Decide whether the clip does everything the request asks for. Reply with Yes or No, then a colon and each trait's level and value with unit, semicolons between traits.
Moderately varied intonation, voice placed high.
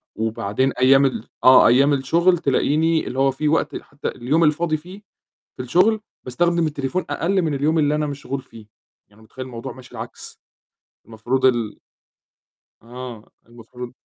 No: average, 4.1 semitones; low, 135 Hz